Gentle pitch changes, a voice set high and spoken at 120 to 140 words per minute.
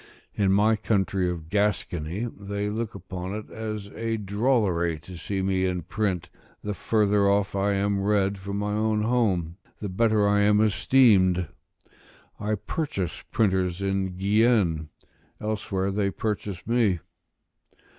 No: narrow, 2.2 semitones; low, 100 Hz; slow, 135 wpm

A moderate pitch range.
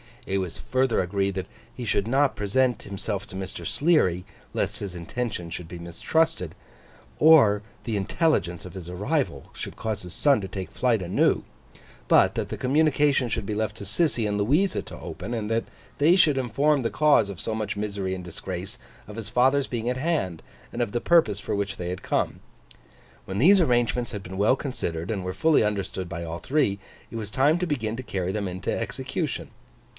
No: wide, 5.8 semitones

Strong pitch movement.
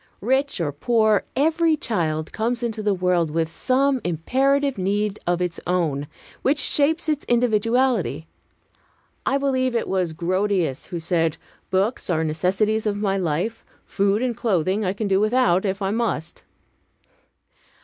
Yes: wide, 5.7 semitones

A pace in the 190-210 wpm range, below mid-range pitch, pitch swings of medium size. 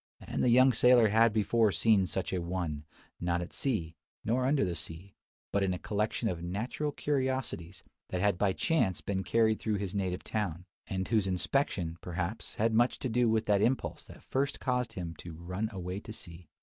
Yes: average, 195 wpm; low, 100 Hz; average, 4.4 semitones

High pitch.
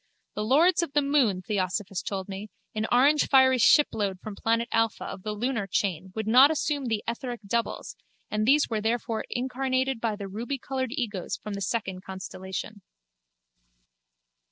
Yes: high, 225 Hz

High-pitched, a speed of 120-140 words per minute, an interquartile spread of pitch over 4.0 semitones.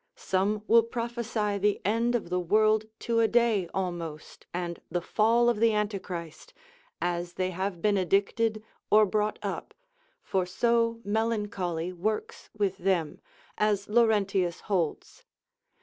No: high, 205 Hz; slow, 135 wpm; average, 3.5 semitones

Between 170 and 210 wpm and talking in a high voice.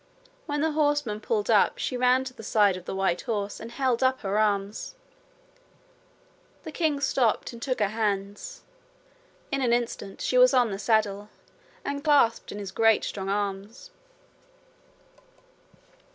No: average, 150 wpm; high, 230 Hz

